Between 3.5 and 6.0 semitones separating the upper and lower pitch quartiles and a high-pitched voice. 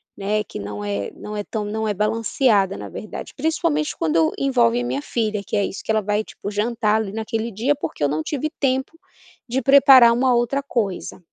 Yes: average, 4.0 semitones; high, 220 Hz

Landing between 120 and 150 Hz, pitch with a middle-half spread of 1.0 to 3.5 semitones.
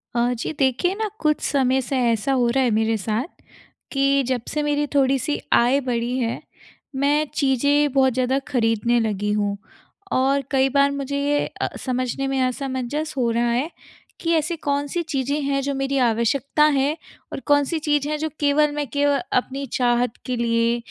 No: very high, 270 Hz; average, 3.0 semitones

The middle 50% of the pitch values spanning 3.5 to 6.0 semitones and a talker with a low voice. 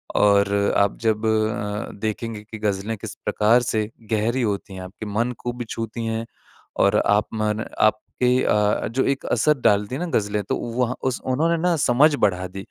No: average, 2.9 semitones; low, 110 Hz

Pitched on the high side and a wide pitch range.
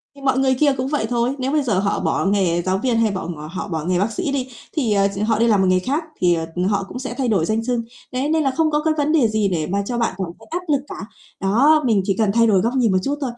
Yes: high, 225 Hz; wide, 5.7 semitones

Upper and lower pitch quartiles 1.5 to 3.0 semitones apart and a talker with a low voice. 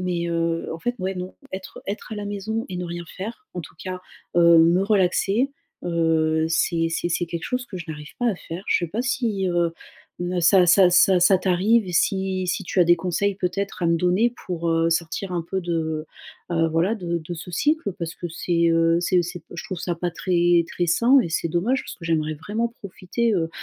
No: narrow, 2.6 semitones; medium, 180 Hz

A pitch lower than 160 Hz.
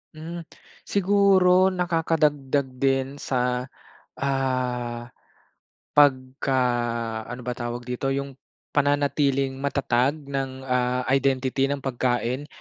Yes: low, 135 Hz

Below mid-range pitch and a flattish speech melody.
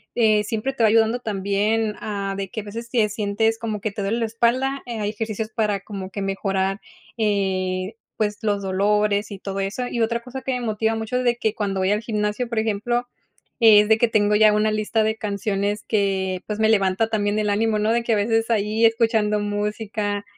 No: high, 210 Hz; narrow, 1.7 semitones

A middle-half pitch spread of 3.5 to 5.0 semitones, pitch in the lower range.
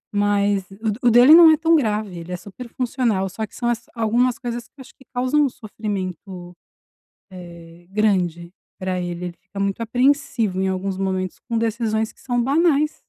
No: average, 4.6 semitones; high, 215 Hz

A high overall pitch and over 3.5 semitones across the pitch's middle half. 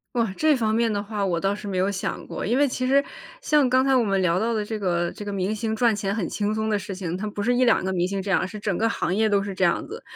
No: high, 210 Hz; average, 3.0 semitones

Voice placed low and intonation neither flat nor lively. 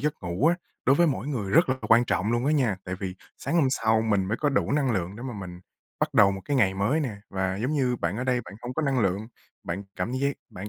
No: low, 115 Hz; wide, 5.8 semitones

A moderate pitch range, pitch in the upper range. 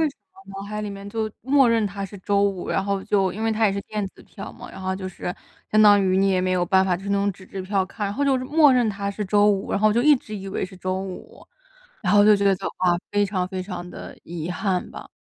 No: narrow, 2.0 semitones; high, 200 Hz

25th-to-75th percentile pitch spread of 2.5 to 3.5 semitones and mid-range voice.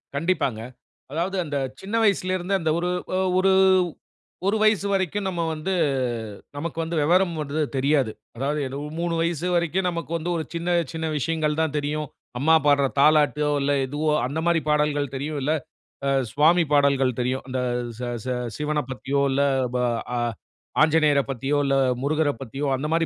Yes: average, 3.1 semitones; medium, 150 Hz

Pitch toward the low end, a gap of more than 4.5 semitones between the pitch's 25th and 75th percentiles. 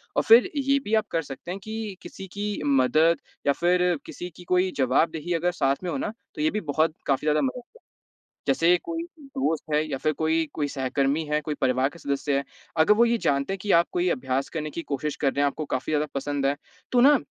No: medium, 160 Hz; average, 4.9 semitones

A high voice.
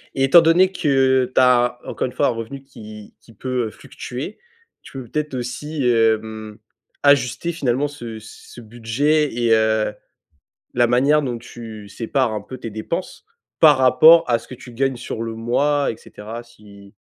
No: low, 125 Hz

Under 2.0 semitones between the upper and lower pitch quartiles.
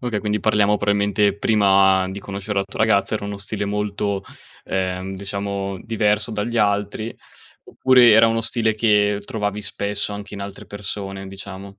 Yes: narrow, 1.3 semitones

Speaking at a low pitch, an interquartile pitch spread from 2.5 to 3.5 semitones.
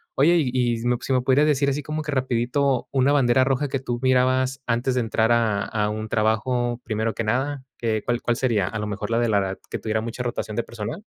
Yes: low, 120 Hz; average, 2.8 semitones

